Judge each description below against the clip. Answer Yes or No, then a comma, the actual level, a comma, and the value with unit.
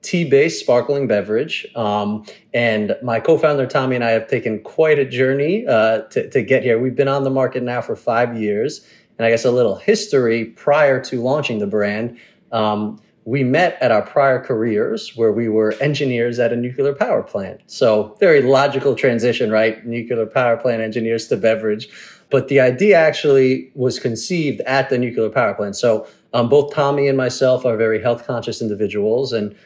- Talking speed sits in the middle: Yes, average, 180 wpm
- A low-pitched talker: Yes, low, 120 Hz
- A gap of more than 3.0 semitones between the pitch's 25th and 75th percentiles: Yes, average, 3.5 semitones